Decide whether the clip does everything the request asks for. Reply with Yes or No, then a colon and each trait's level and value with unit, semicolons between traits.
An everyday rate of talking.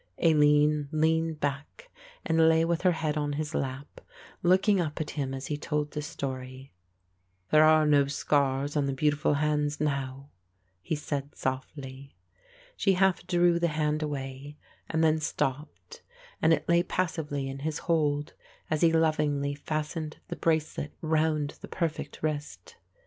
Yes: average, 150 wpm